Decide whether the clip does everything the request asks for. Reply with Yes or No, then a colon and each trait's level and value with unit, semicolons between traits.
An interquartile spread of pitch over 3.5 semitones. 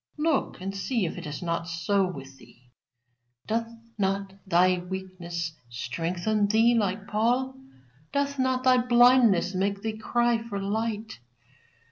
Yes: average, 4.7 semitones